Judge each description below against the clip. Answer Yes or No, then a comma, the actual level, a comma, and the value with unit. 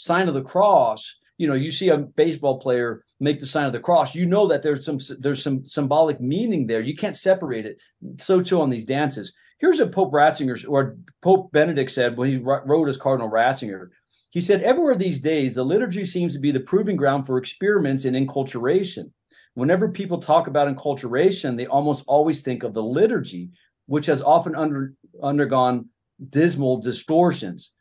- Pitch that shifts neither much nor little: Yes, average, 4.5 semitones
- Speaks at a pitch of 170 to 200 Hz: No, medium, 145 Hz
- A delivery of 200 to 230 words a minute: No, average, 185 wpm